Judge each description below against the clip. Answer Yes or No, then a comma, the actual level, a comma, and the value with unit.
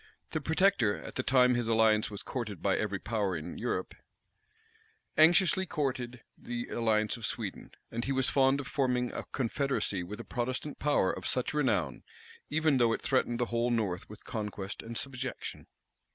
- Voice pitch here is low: Yes, low, 120 Hz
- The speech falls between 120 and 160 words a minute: No, average, 170 wpm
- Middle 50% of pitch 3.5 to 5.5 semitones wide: Yes, average, 3.9 semitones